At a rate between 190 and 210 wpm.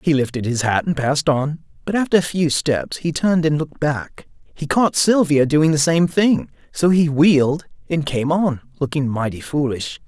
Yes: average, 195 wpm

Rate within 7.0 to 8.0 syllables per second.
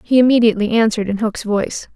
Yes: 7.1 syllables/s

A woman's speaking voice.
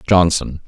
No: male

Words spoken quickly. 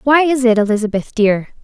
No: average, 185 wpm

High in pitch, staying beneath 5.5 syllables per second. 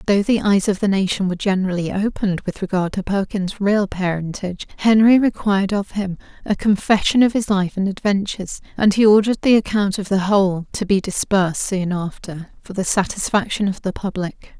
No: high, 195 Hz; 5.6 syllables/s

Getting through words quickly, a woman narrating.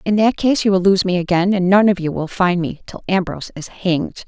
Yes: fast, 265 wpm; female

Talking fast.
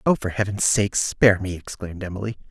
No: average, 190 wpm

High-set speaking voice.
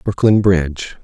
No: very low, 95 Hz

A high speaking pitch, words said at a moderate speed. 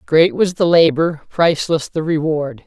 No: medium, 155 Hz; average, 160 wpm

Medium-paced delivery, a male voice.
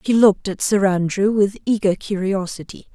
No: average, 165 wpm; female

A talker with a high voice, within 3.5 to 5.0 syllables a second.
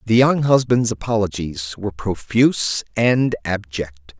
No: low, 105 Hz; 4.2 syllables/s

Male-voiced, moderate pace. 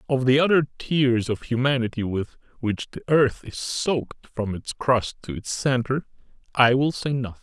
Yes: male; average, 180 wpm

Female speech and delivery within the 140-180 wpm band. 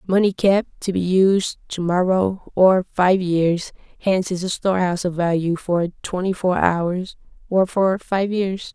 Yes: female; average, 165 wpm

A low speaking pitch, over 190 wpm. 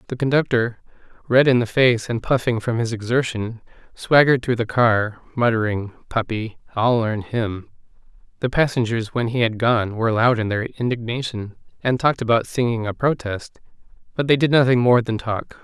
No: low, 120 Hz; average, 170 wpm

